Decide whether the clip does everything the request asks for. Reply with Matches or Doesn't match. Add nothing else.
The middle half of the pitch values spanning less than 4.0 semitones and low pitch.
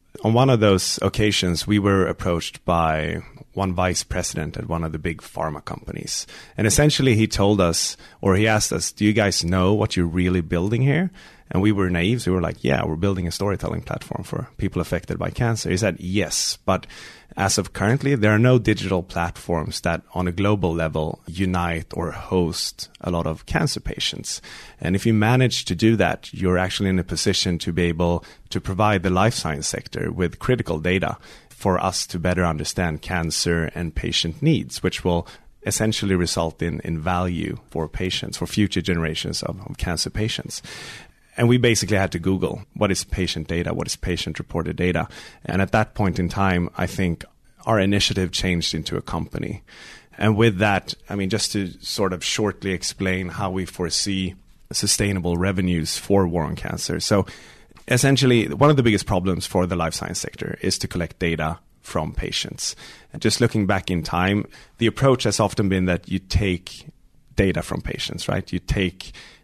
Matches